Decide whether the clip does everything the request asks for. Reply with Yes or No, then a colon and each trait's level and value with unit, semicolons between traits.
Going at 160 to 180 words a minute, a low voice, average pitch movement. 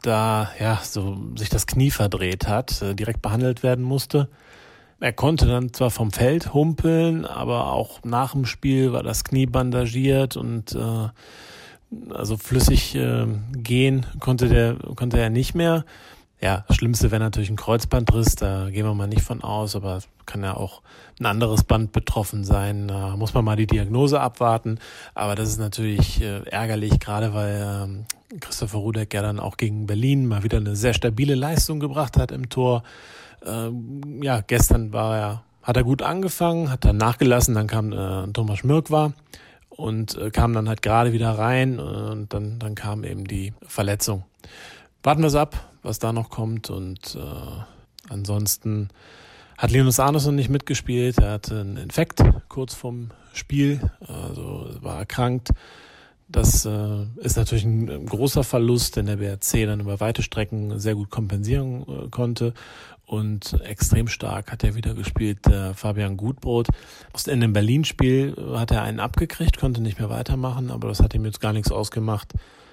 Yes: average, 165 wpm; low, 115 Hz; average, 3.2 semitones